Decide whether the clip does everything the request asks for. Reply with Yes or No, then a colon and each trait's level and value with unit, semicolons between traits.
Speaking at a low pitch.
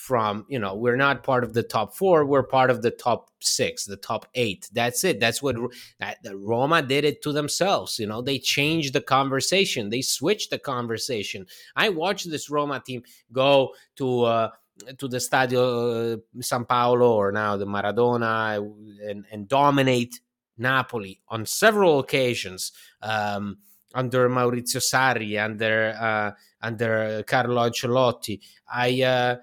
Yes: low, 120 Hz